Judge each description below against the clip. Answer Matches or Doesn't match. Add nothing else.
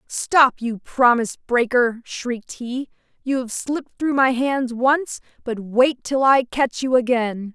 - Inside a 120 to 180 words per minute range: Matches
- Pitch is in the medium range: Doesn't match